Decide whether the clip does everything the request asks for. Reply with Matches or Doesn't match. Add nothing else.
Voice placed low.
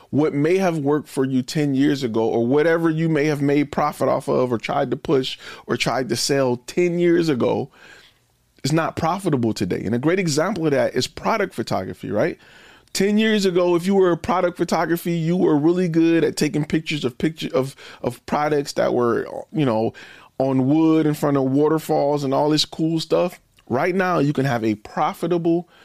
Doesn't match